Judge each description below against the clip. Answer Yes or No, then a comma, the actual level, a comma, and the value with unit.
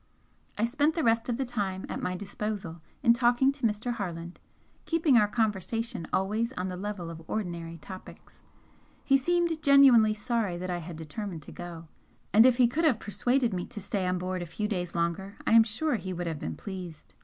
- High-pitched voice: Yes, high, 210 Hz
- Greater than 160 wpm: Yes, average, 200 wpm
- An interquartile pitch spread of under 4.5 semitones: No, average, 5.1 semitones